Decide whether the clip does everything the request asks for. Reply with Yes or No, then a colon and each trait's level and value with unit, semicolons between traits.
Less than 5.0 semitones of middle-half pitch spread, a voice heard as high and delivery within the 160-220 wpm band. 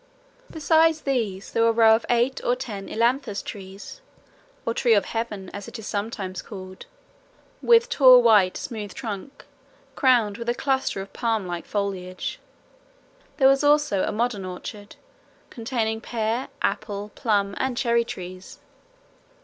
No: average, 3.8 semitones; high, 225 Hz; average, 145 wpm